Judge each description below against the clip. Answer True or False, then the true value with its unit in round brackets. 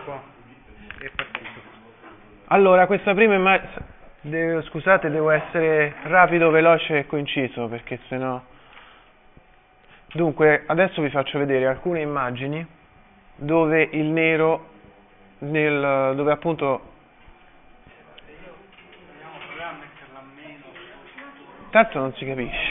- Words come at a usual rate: False (80 wpm)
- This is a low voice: False (155 Hz)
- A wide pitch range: False (3.1 semitones)